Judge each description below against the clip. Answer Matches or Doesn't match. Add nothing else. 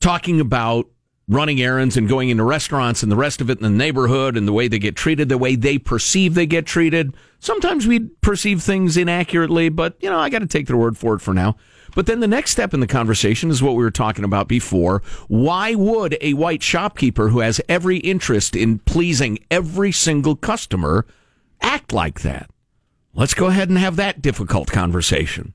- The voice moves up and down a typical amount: Doesn't match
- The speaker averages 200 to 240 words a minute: Matches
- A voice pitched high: Doesn't match